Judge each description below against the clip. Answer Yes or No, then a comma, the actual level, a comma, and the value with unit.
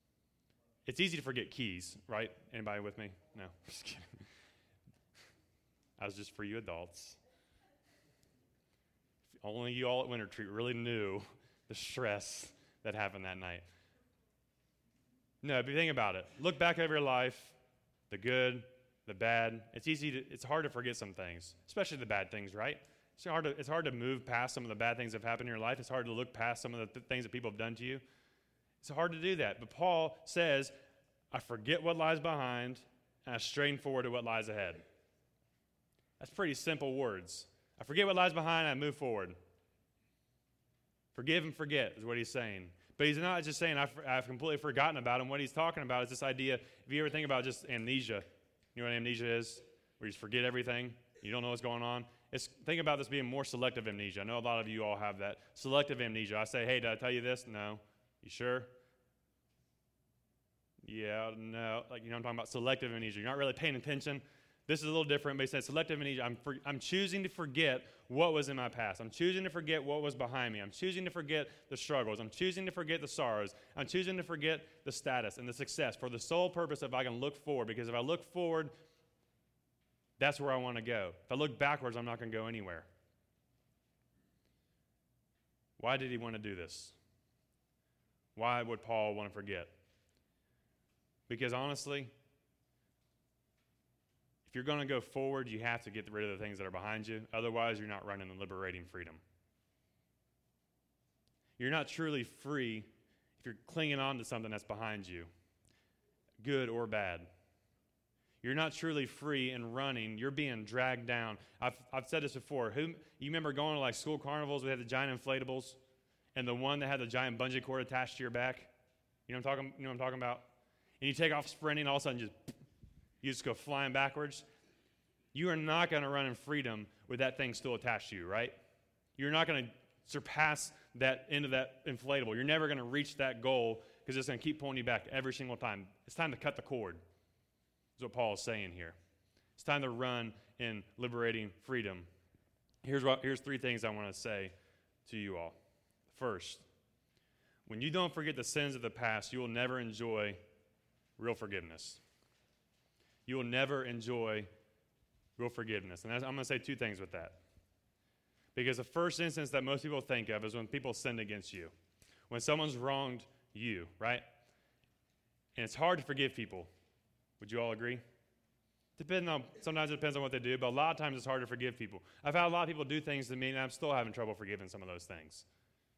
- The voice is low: Yes, low, 125 Hz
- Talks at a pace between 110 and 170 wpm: No, fast, 205 wpm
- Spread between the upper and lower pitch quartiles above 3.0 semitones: Yes, average, 4.2 semitones